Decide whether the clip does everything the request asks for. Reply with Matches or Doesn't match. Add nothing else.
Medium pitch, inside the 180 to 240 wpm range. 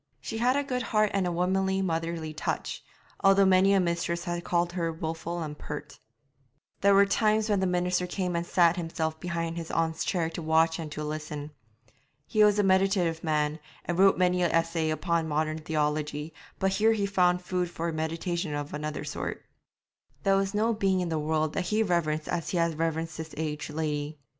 Matches